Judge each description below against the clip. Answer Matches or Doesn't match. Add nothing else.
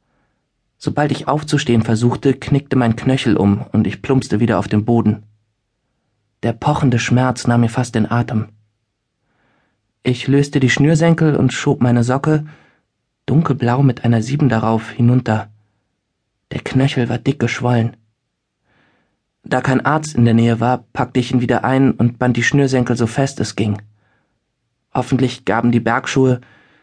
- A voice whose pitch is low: Matches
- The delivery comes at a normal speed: Matches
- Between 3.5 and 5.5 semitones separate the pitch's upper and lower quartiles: Doesn't match